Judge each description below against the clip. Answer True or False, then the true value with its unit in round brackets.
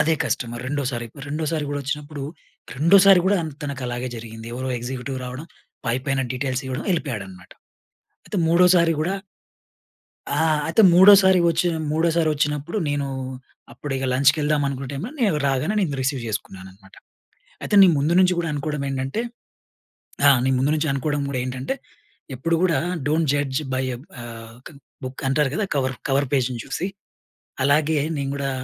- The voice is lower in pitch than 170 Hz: True (140 Hz)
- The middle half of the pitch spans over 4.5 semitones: False (3.8 semitones)